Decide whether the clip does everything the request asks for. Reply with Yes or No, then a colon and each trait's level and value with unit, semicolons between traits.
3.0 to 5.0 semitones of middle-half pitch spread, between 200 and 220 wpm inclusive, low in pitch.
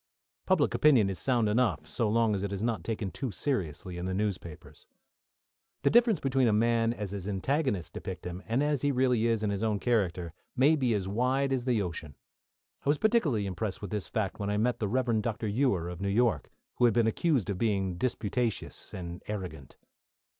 Yes: average, 4.5 semitones; fast, 205 wpm; low, 110 Hz